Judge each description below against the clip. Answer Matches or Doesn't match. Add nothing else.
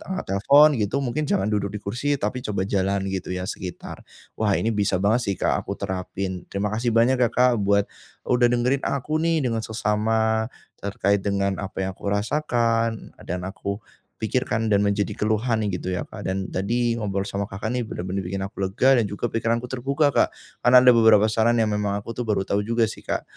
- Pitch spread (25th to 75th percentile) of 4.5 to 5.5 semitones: Doesn't match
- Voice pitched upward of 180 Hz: Doesn't match